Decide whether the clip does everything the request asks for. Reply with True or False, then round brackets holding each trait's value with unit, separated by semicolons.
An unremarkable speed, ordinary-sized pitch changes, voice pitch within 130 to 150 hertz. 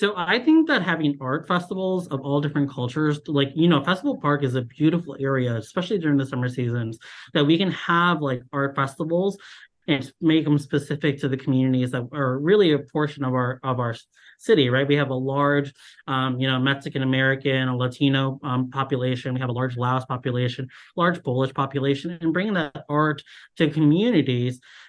True (190 wpm; 3.5 semitones; 140 Hz)